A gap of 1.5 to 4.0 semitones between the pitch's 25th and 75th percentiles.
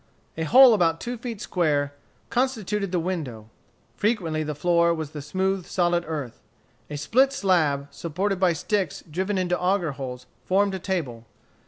No: average, 4.7 semitones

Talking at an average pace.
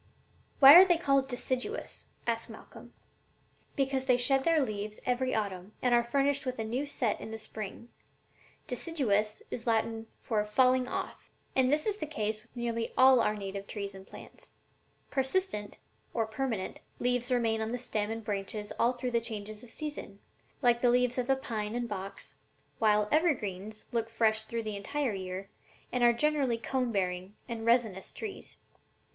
Yes: average, 175 wpm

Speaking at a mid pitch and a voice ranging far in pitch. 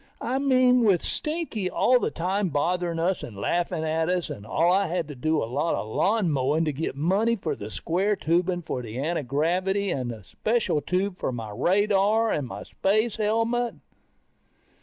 Yes: medium, 175 Hz; wide, 5.8 semitones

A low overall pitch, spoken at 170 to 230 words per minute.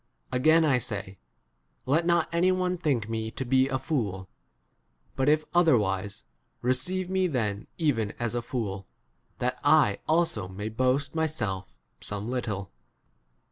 No: low, 130 Hz; average, 145 wpm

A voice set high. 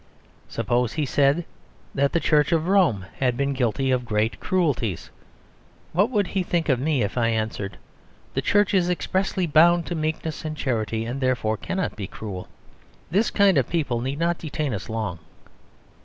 No: medium, 140 Hz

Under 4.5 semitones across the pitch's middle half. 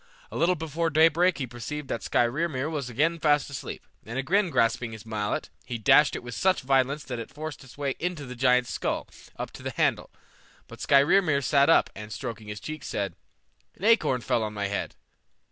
No: average, 4.8 semitones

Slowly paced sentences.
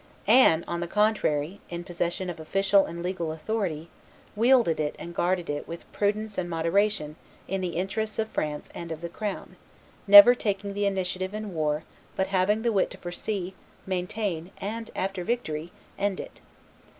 No: average, 165 wpm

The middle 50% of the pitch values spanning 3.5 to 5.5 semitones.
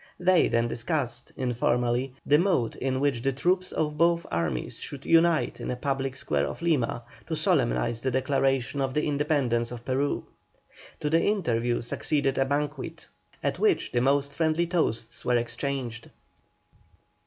Yes: average, 4.0 semitones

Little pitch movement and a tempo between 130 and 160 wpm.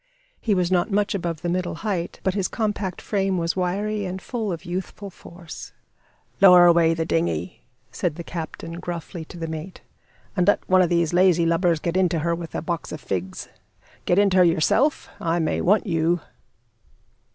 No: narrow, 2.3 semitones; average, 185 wpm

